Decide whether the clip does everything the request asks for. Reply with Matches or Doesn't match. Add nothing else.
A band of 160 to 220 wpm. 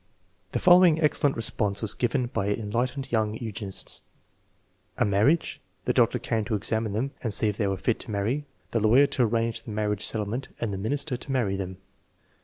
Matches